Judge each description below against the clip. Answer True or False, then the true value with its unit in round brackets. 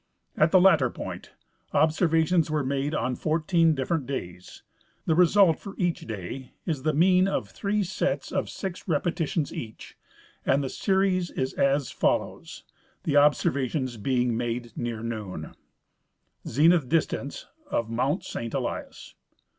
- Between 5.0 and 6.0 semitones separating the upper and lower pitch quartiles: True (5.3 semitones)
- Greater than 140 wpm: False (135 wpm)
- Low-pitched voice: False (145 Hz)